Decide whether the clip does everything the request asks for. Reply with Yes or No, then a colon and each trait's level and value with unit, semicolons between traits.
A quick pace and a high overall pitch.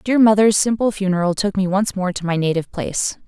Yes: fast, 220 wpm; high, 195 Hz